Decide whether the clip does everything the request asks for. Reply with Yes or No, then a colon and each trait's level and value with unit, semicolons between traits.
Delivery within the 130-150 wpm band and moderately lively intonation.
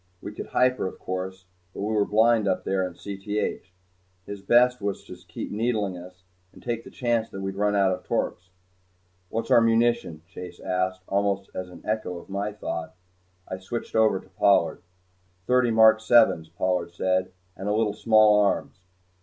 No: average, 180 wpm; average, 3.1 semitones